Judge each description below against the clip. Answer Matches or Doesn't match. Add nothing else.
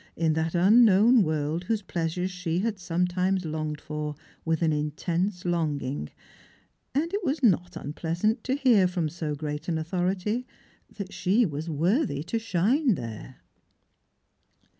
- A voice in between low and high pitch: Matches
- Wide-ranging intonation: Doesn't match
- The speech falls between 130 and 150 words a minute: Matches